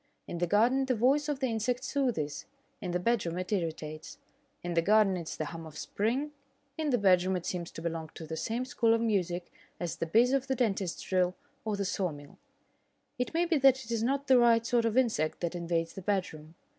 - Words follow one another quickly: Yes, fast, 225 wpm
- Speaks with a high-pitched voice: Yes, high, 205 Hz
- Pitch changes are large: Yes, wide, 6.4 semitones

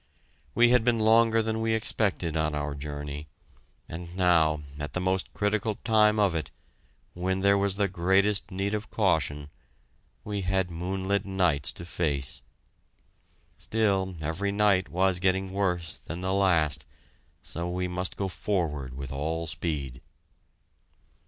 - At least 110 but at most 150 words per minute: Yes, average, 140 wpm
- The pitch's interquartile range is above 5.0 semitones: No, average, 3.8 semitones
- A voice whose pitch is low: Yes, very low, 95 Hz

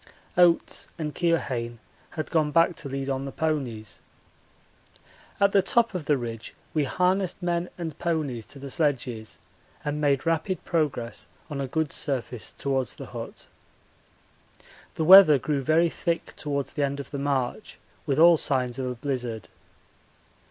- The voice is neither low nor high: Yes, medium, 145 Hz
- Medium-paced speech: Yes, average, 155 wpm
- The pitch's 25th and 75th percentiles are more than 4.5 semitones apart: No, average, 4.1 semitones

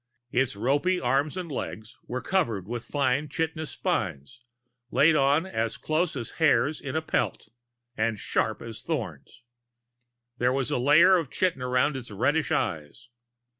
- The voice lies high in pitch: No, low, 135 Hz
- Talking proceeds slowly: No, average, 150 wpm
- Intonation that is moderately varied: Yes, average, 4.8 semitones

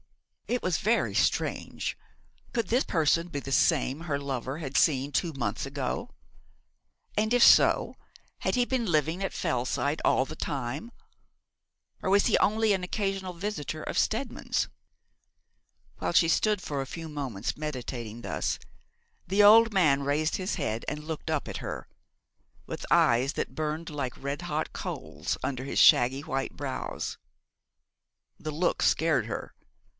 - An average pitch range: No, wide, 5.7 semitones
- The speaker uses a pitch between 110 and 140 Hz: No, medium, 155 Hz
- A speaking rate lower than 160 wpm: Yes, average, 150 wpm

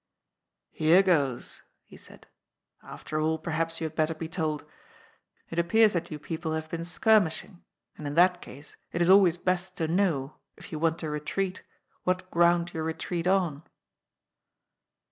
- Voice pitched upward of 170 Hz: No, medium, 165 Hz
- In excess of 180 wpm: No, average, 170 wpm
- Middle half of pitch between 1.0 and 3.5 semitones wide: Yes, narrow, 2.4 semitones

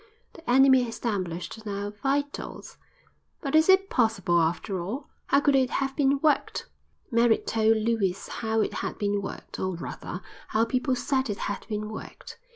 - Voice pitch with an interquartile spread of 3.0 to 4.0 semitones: No, average, 4.9 semitones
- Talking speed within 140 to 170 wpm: Yes, average, 165 wpm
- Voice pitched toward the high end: Yes, high, 225 Hz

